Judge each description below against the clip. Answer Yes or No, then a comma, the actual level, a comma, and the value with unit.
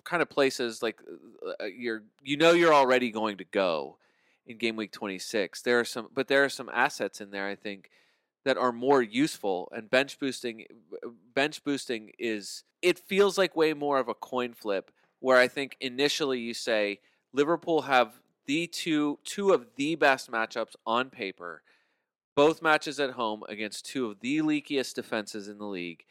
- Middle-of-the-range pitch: No, low, 130 Hz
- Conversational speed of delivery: Yes, average, 175 wpm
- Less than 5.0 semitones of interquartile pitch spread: No, wide, 5.5 semitones